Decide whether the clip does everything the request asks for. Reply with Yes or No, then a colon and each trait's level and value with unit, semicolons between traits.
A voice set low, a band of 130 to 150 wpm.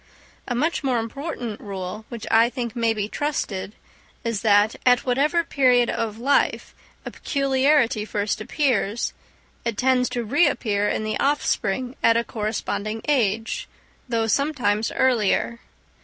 No: high, 235 Hz; slow, 135 wpm